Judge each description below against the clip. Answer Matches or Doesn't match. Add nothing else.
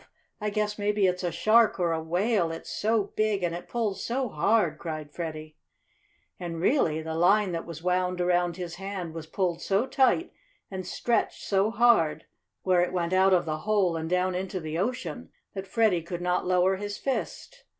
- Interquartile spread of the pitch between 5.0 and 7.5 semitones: Doesn't match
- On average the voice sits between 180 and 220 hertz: Matches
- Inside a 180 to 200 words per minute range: Matches